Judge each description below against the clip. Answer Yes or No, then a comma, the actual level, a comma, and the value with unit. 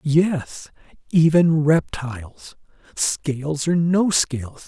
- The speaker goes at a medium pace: No, slow, 90 wpm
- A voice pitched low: No, medium, 150 Hz